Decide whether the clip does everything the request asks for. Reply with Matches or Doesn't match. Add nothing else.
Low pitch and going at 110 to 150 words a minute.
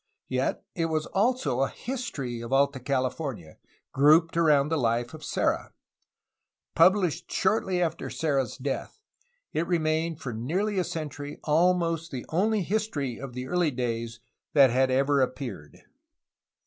Doesn't match